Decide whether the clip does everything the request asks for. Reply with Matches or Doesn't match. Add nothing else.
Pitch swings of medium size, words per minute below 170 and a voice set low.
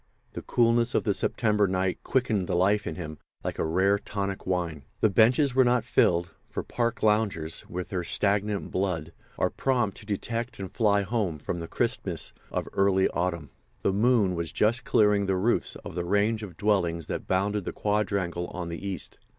Doesn't match